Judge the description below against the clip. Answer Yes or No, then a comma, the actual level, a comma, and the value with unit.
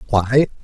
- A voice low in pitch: Yes, low, 120 Hz